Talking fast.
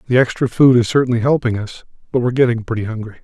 Yes: fast, 240 wpm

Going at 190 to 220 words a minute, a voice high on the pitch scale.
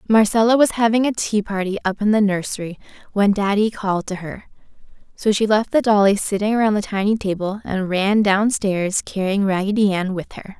Yes: average, 195 wpm; high, 205 Hz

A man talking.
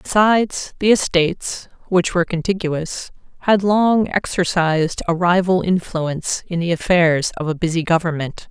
No: female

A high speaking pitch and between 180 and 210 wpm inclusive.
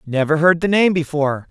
No: medium, 160 Hz; average, 200 wpm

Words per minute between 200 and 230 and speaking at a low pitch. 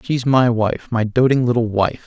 Yes: fast, 205 wpm; low, 120 Hz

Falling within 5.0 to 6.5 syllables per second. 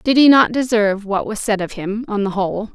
Yes: 5.8 syllables/s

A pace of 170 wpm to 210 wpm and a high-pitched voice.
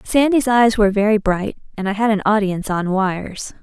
Yes: average, 200 wpm; high, 210 Hz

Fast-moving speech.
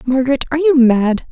No: average, 180 wpm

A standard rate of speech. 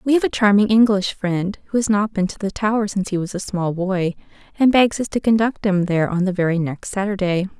No: fast, 245 wpm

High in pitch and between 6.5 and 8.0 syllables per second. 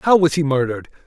No: medium, 150 Hz; 7.6 syllables/s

